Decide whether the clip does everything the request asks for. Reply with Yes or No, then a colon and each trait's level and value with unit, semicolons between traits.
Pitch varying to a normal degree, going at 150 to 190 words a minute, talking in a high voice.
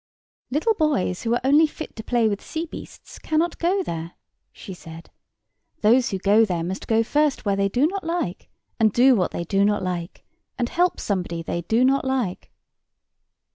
No: wide, 7.9 semitones; average, 185 wpm; high, 225 Hz